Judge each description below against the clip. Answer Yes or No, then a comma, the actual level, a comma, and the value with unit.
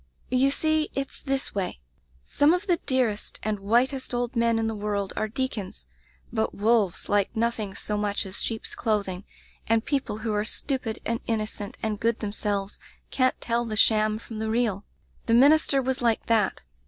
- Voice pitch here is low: No, high, 225 Hz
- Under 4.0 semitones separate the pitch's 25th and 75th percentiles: Yes, average, 3.4 semitones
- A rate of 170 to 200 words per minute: Yes, average, 180 wpm